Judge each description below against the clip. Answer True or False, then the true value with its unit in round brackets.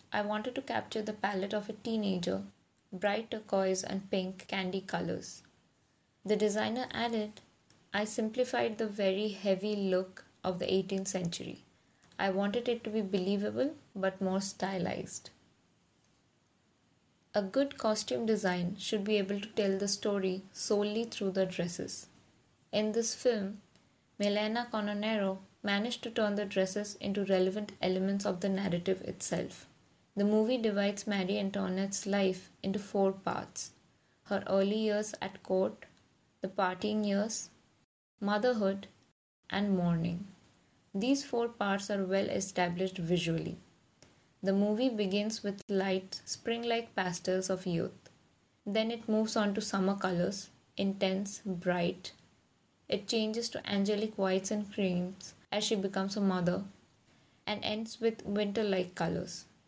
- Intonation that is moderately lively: False (2.1 semitones)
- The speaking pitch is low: False (200 Hz)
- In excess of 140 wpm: False (135 wpm)